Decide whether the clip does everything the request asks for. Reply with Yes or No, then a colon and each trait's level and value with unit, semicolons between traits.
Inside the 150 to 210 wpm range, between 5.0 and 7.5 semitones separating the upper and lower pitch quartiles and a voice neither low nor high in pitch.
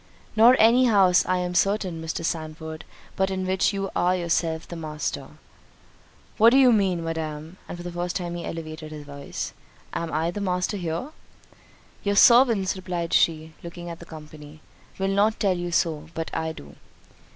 No: average, 175 wpm; average, 3.2 semitones; medium, 175 Hz